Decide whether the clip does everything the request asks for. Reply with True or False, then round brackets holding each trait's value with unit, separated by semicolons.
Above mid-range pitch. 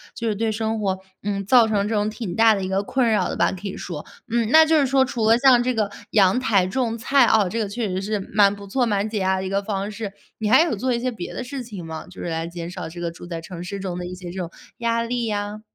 True (210 Hz)